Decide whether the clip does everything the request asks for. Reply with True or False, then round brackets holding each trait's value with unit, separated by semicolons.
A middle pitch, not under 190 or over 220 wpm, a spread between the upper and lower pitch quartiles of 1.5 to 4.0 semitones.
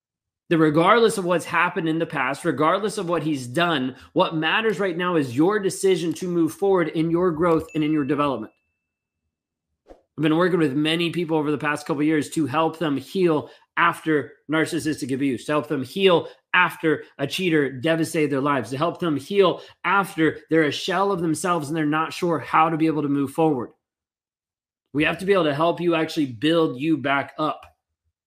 True (160 Hz; 195 wpm; 2.6 semitones)